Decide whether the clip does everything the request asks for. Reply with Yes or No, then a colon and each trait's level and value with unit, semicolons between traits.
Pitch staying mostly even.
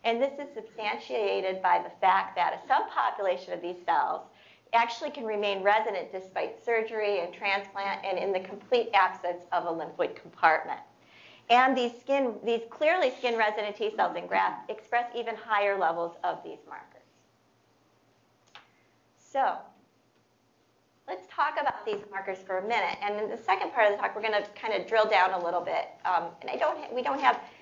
No: average, 3.7 semitones